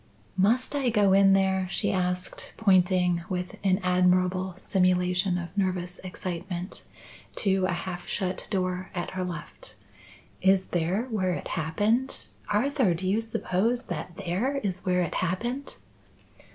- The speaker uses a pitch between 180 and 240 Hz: Yes, medium, 185 Hz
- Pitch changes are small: Yes, narrow, 1.7 semitones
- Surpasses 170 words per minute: No, average, 140 wpm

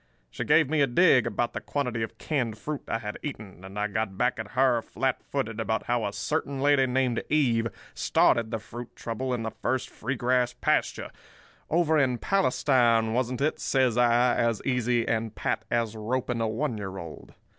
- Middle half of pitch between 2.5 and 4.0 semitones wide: Yes, average, 2.8 semitones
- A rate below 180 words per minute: No, average, 190 wpm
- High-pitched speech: No, low, 120 Hz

